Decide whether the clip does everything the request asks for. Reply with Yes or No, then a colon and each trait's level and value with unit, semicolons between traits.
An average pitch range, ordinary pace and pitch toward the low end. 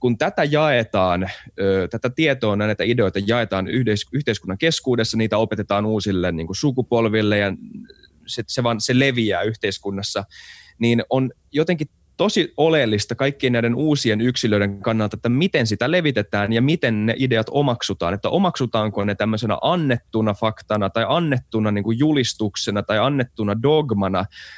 Yes: average, 3.7 semitones; average, 135 wpm; low, 115 Hz